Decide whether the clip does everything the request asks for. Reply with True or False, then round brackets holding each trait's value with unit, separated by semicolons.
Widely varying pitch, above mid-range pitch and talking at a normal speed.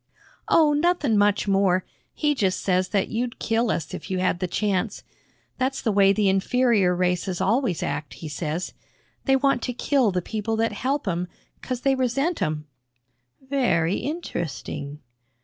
True (6.0 semitones; 205 Hz; 160 wpm)